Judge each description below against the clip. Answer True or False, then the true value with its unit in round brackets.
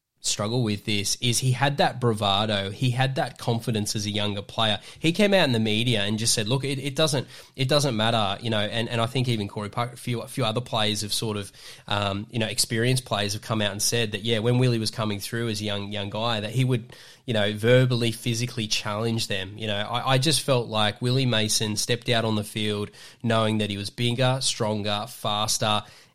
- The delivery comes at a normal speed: False (235 wpm)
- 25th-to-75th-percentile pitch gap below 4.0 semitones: True (2.8 semitones)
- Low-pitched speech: True (115 Hz)